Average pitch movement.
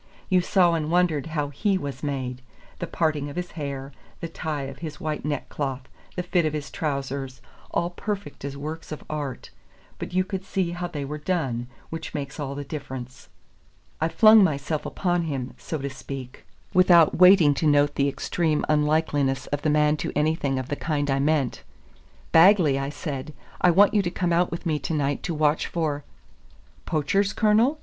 Yes: average, 3.6 semitones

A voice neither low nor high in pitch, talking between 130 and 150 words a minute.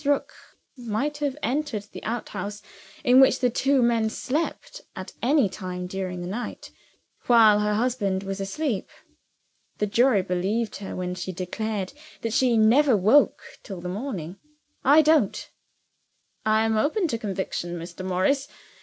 No: high, 220 Hz; average, 145 wpm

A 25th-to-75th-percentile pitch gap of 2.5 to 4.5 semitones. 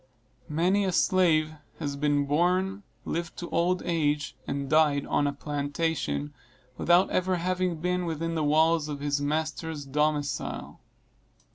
Yes: average, 3.0 semitones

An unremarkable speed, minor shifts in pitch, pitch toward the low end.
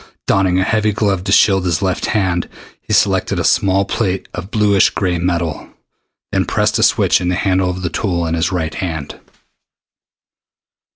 Yes: average, 175 wpm; narrow, 1.9 semitones; very low, 95 Hz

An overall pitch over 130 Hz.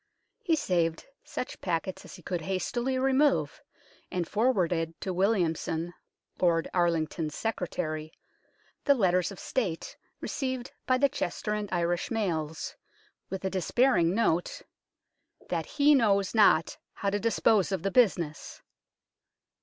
Yes: high, 190 Hz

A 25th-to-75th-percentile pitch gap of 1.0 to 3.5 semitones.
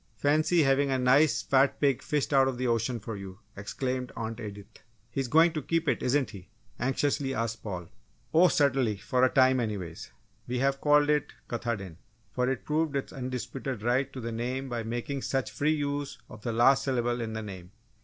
Yes: average, 3.2 semitones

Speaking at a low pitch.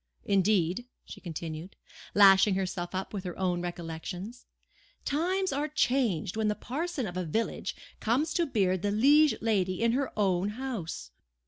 No: high, 205 Hz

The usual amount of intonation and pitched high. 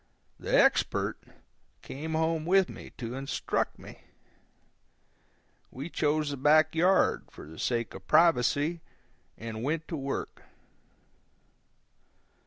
No: average, 3.9 semitones; medium, 150 Hz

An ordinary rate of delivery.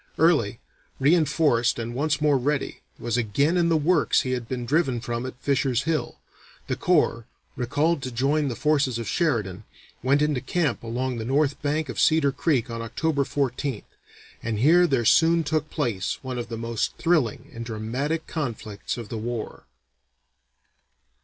Yes: average, 165 wpm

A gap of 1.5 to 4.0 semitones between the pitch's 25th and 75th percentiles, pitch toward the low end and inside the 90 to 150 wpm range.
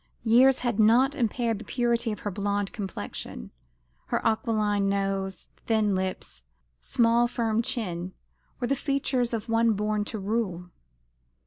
No: average, 3.1 semitones; high, 220 Hz; slow, 135 wpm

